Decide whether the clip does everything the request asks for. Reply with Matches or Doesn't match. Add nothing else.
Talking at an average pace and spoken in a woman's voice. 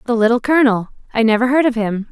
Doesn't match